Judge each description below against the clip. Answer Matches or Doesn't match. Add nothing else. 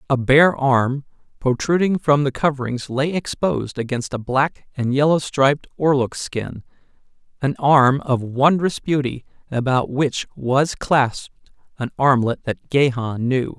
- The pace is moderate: Doesn't match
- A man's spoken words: Matches